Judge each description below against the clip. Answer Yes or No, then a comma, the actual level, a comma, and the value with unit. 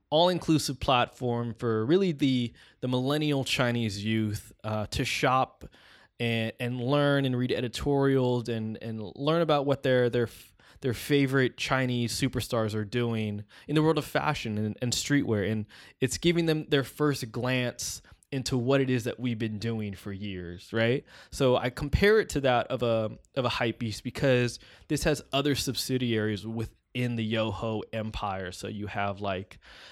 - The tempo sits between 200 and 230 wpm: No, average, 160 wpm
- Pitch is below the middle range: Yes, low, 125 Hz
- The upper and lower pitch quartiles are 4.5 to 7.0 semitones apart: No, average, 3.9 semitones